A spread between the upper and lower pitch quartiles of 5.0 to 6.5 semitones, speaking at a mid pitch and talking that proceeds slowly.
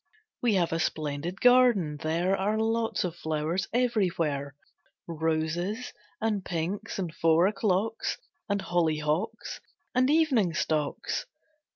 Yes: wide, 5.6 semitones; medium, 180 Hz; slow, 110 wpm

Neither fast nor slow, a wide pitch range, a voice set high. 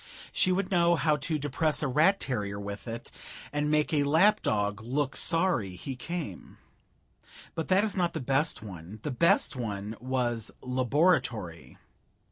No: average, 155 wpm; wide, 7.0 semitones; low, 135 Hz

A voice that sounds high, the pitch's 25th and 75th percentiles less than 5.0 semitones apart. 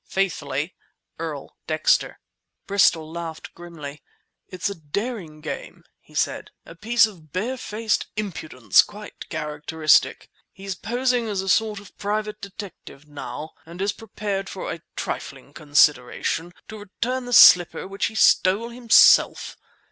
No: high, 195 Hz; average, 5.3 semitones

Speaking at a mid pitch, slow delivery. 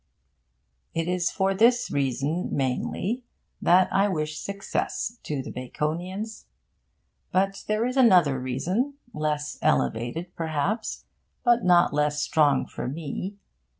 Yes: medium, 175 Hz; slow, 115 wpm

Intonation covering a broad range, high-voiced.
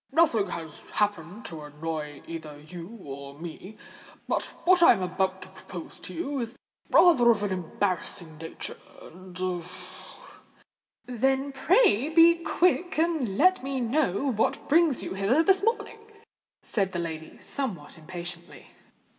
Yes: wide, 8.3 semitones; high, 200 Hz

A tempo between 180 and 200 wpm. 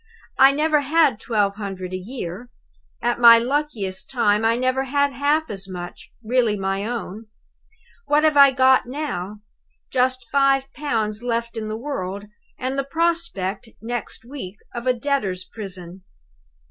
No: average, 145 wpm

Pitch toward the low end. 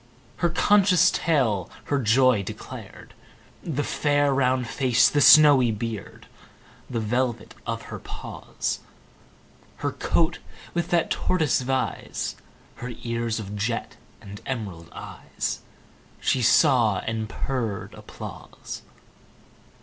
Yes: low, 125 Hz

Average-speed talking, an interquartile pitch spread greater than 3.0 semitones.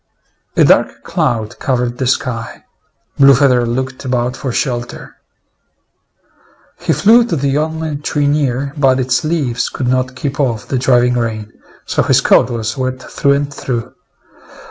No: average, 150 wpm; narrow, 2.5 semitones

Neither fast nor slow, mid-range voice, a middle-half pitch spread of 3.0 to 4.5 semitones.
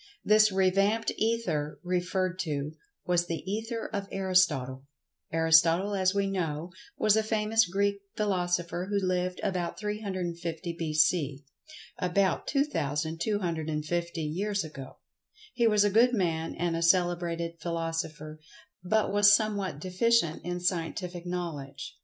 No: slow, 115 wpm; medium, 180 Hz; average, 3.5 semitones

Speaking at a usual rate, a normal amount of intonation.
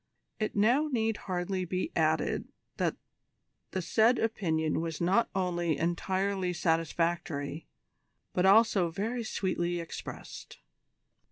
No: slow, 105 wpm; average, 4.2 semitones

